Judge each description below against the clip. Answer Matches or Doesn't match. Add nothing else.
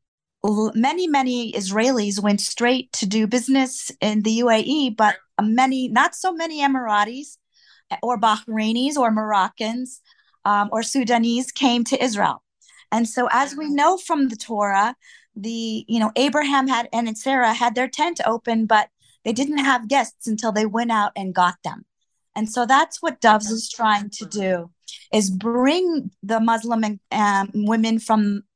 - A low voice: Doesn't match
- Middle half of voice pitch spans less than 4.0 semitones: Matches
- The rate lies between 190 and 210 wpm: Doesn't match